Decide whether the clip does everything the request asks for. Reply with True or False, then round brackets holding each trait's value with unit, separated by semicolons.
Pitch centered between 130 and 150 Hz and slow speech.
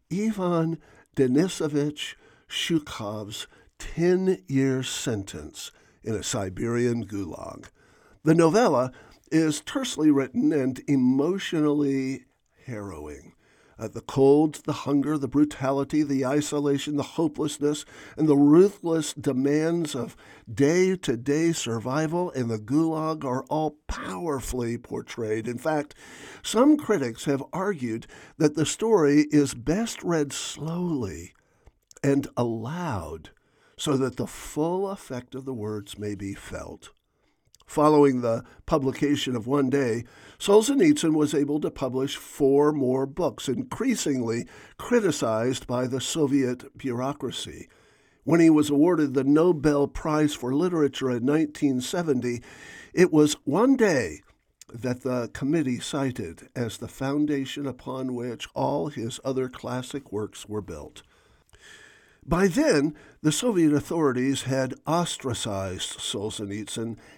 True (140 Hz; 115 wpm)